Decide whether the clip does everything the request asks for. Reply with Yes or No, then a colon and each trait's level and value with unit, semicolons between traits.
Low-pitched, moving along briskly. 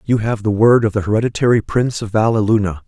Yes: low, 110 Hz; fast, 210 wpm